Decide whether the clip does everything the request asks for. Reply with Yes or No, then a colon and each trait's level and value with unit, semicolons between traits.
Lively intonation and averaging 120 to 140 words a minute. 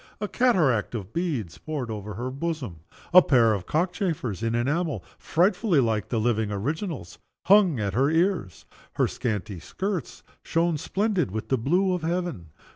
No: wide, 8.2 semitones; average, 160 wpm